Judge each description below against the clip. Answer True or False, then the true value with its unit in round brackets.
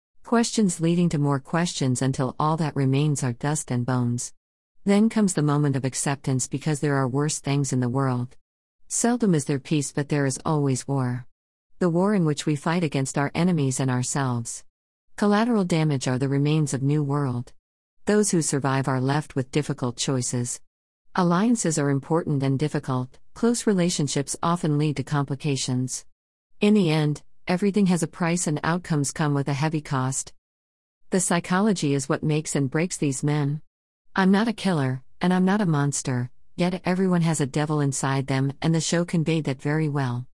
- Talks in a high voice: False (145 Hz)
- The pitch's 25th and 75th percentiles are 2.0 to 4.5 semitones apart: True (3.8 semitones)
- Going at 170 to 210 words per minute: True (180 wpm)